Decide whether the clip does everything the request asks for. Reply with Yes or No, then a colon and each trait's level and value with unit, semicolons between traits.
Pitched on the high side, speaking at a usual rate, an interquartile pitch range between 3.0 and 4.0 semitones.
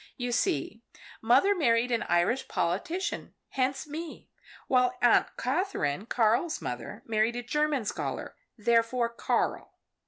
No: high, 245 Hz; slow, 120 wpm; average, 3.5 semitones